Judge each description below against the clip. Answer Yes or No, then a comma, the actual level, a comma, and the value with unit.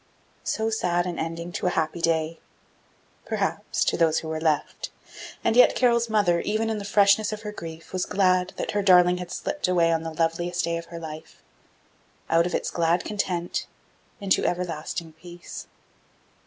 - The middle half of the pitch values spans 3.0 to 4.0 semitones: Yes, average, 3.3 semitones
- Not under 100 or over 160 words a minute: No, average, 175 wpm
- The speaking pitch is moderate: Yes, medium, 175 Hz